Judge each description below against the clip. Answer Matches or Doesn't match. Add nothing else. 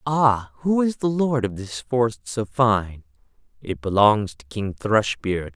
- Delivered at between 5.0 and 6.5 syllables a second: Doesn't match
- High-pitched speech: Doesn't match